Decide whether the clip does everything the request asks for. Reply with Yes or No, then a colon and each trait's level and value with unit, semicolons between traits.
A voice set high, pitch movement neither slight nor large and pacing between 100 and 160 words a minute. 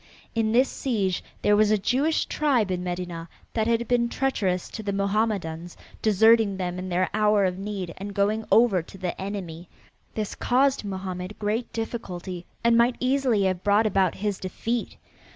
No: high, 205 Hz; average, 3.6 semitones; average, 170 wpm